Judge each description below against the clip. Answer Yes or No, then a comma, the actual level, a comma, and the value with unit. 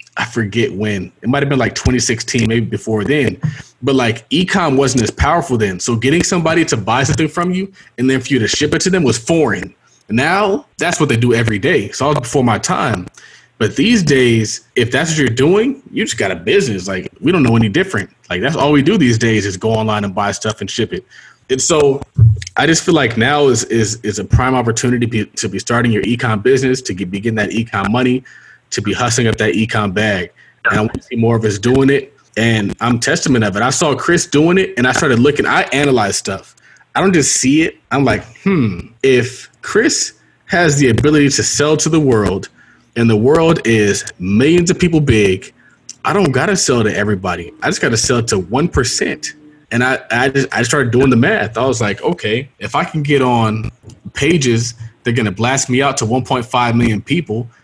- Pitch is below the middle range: Yes, low, 125 Hz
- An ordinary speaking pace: No, fast, 225 wpm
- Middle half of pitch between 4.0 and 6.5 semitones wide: Yes, average, 4.6 semitones